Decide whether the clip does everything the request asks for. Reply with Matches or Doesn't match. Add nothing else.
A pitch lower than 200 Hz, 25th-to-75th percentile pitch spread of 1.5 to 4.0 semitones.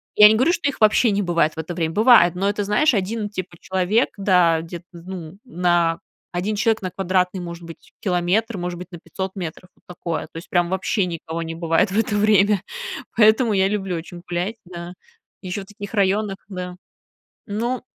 Matches